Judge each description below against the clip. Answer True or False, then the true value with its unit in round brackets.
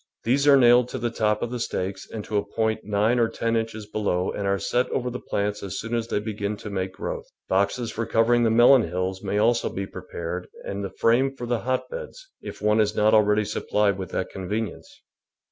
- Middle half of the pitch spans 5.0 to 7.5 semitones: False (2.9 semitones)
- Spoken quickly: True (225 wpm)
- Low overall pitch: True (110 Hz)